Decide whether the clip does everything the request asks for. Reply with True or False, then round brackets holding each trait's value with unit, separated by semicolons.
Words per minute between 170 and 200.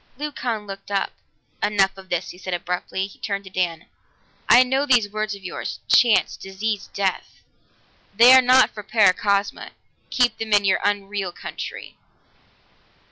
False (150 wpm)